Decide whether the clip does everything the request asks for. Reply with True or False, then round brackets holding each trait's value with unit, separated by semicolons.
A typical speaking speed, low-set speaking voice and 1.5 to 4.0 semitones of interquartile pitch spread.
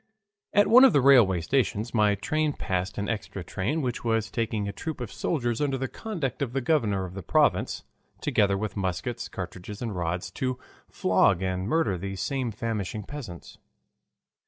False (175 wpm; 110 Hz; 5.6 semitones)